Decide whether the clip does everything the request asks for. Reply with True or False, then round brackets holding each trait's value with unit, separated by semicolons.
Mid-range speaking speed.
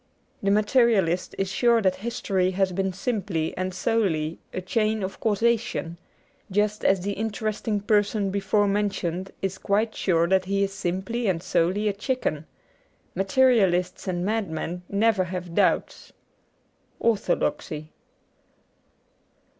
False (125 wpm)